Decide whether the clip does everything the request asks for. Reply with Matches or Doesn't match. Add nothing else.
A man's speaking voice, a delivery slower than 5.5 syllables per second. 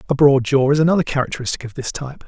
Doesn't match